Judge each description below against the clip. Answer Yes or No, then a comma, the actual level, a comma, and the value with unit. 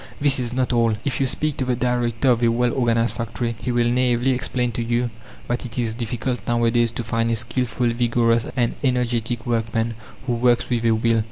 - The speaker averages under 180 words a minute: No, fast, 205 wpm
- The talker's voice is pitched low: Yes, low, 120 Hz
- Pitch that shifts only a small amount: Yes, narrow, 1.2 semitones